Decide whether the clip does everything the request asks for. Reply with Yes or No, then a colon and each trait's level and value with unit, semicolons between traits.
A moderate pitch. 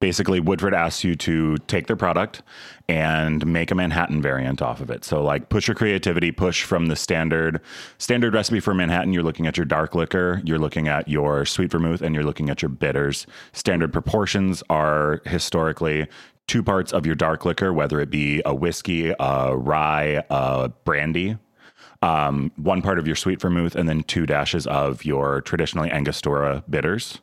No: very low, 80 Hz